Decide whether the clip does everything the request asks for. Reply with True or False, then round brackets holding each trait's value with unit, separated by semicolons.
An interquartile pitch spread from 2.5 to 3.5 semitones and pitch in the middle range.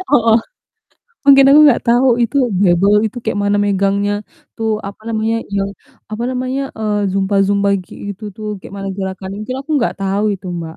False (2.9 semitones; 205 Hz)